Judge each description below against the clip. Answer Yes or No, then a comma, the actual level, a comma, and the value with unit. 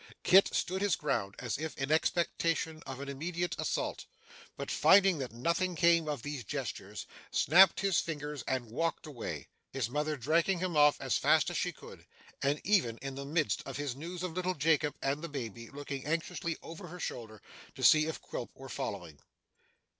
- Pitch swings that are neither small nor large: Yes, average, 4.0 semitones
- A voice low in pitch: No, medium, 150 Hz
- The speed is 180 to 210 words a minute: Yes, average, 185 wpm